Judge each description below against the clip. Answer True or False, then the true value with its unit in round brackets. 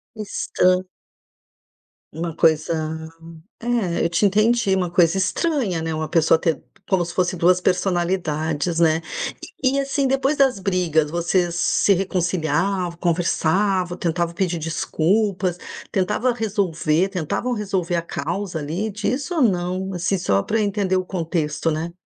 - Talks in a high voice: False (180 Hz)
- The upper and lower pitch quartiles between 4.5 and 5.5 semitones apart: False (3.2 semitones)